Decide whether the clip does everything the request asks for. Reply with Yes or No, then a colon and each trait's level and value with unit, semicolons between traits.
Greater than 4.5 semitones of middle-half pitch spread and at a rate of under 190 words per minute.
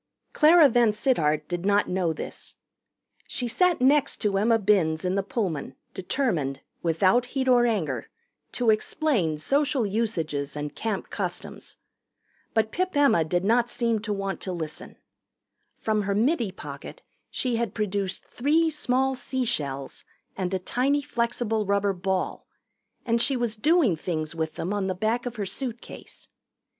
Yes: average, 5.3 semitones; average, 150 wpm